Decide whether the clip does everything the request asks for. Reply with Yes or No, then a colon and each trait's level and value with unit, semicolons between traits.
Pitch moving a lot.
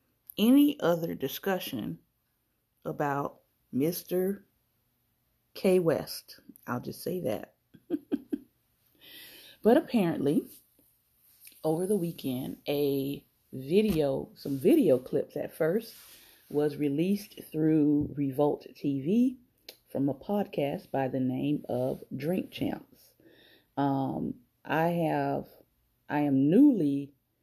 Yes: wide, 6.5 semitones